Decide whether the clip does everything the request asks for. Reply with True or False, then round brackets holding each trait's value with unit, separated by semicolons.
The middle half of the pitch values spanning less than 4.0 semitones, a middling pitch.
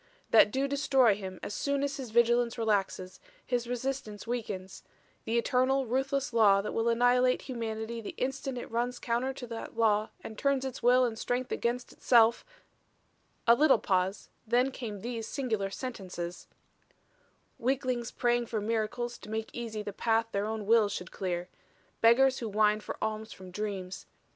False (2.8 semitones; 230 Hz)